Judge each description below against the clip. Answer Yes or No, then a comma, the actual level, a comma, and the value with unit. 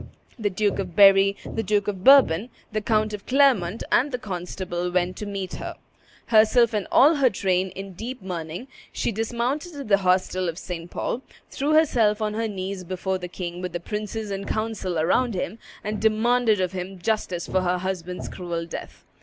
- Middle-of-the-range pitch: No, high, 200 Hz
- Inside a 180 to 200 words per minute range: Yes, average, 185 wpm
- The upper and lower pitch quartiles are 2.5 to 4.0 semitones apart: Yes, average, 3.5 semitones